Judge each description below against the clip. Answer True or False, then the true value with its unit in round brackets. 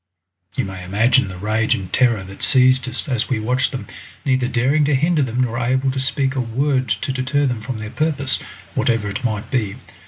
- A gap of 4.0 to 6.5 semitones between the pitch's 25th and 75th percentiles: False (3.3 semitones)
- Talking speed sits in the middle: False (210 wpm)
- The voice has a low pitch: True (125 Hz)